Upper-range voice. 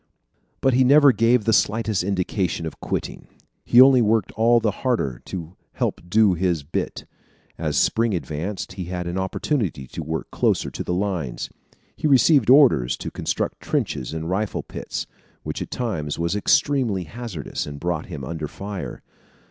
No: very low, 95 Hz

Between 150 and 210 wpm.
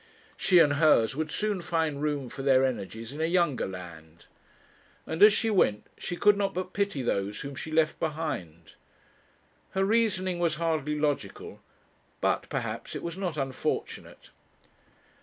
Yes: average, 155 wpm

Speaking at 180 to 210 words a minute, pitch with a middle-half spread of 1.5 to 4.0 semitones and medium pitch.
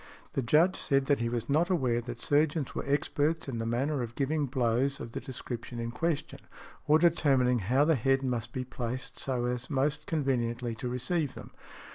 No: average, 190 wpm; average, 3.4 semitones; low, 130 Hz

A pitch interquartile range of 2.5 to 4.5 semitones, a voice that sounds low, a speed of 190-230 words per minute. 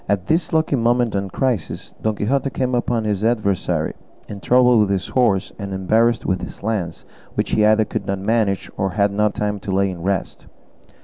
Yes: average, 3.3 semitones; low, 105 Hz; average, 195 wpm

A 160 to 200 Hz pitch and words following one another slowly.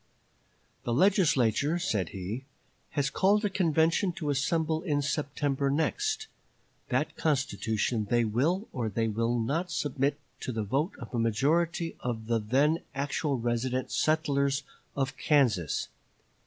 No: medium, 140 Hz; slow, 130 wpm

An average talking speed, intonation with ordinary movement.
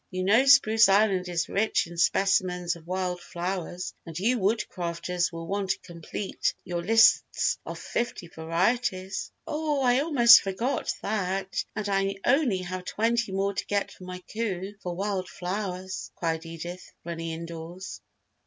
Yes: average, 150 wpm; average, 3.4 semitones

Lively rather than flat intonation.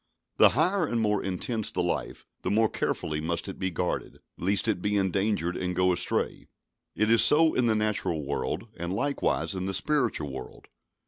No: average, 4.2 semitones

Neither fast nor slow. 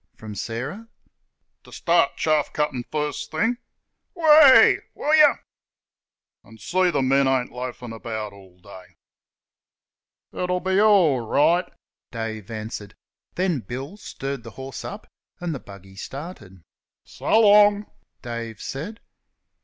No: slow, 120 wpm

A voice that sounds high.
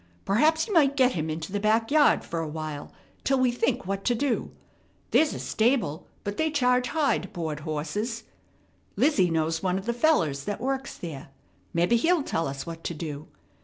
Yes: high, 205 Hz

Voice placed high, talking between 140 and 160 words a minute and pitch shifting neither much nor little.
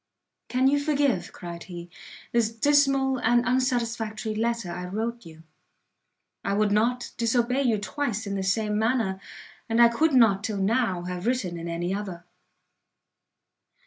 Yes: high, 225 Hz; average, 145 wpm; average, 4.4 semitones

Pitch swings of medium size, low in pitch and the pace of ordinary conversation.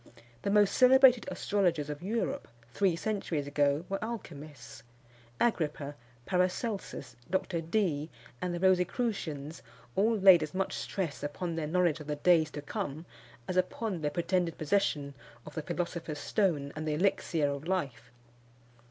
No: average, 4.6 semitones; medium, 170 Hz; average, 145 wpm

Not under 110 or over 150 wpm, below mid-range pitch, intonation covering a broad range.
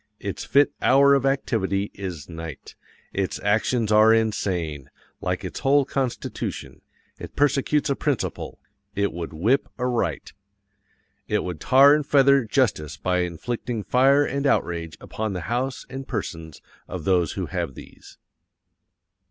Yes: average, 140 wpm; low, 110 Hz; wide, 7.2 semitones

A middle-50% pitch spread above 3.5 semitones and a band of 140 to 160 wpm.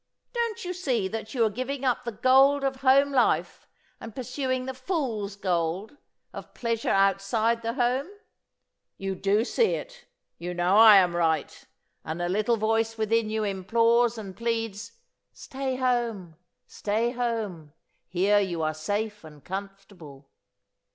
Yes: average, 4.5 semitones; average, 145 wpm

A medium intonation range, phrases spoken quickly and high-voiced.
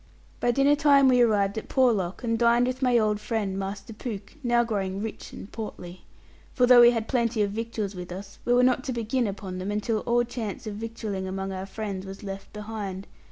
Yes: average, 3.5 semitones; fast, 210 wpm; high, 220 Hz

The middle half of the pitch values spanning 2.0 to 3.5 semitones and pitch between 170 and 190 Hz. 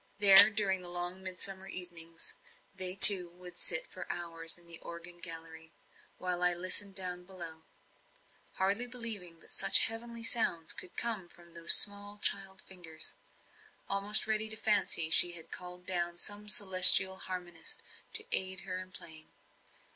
Yes: average, 2.7 semitones; medium, 185 Hz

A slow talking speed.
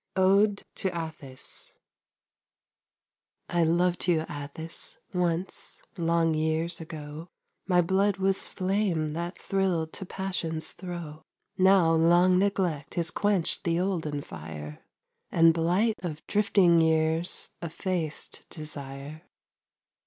Yes: slow, 105 wpm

